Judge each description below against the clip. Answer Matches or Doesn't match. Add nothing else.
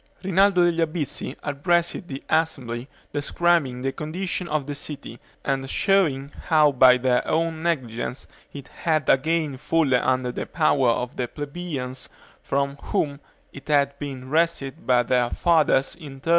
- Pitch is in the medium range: Matches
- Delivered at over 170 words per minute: Doesn't match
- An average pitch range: Matches